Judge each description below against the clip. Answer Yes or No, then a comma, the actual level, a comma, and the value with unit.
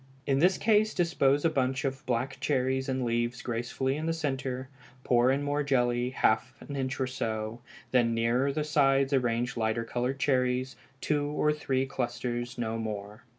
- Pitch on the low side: Yes, low, 130 Hz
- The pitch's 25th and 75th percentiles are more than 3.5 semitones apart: No, narrow, 2.4 semitones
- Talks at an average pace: Yes, average, 170 wpm